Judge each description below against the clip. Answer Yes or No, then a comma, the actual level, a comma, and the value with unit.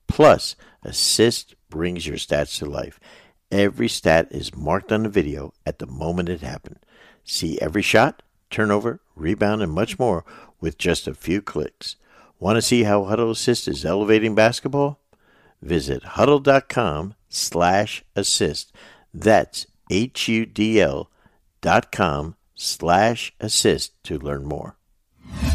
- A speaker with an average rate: No, slow, 115 wpm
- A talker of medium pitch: No, very low, 95 Hz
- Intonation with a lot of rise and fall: Yes, wide, 5.8 semitones